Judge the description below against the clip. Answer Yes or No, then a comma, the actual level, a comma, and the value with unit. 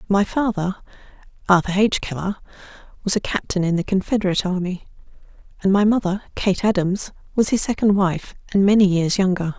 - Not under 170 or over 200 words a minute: No, average, 155 wpm